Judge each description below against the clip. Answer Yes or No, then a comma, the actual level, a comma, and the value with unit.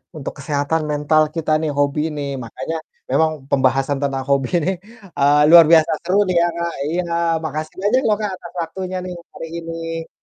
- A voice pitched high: No, medium, 160 Hz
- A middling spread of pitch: Yes, average, 3.0 semitones